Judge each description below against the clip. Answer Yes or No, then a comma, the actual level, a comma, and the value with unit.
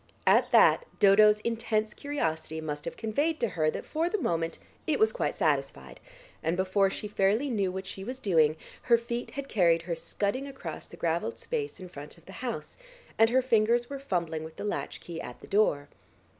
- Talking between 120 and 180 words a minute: No, average, 200 wpm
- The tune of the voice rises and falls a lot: Yes, wide, 6.5 semitones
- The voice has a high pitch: Yes, high, 205 Hz